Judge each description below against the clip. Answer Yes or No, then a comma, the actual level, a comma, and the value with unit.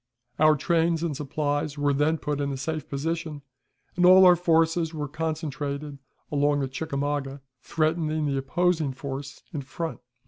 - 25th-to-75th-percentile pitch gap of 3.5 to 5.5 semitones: No, narrow, 2.5 semitones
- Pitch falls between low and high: Yes, medium, 150 Hz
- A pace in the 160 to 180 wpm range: No, average, 150 wpm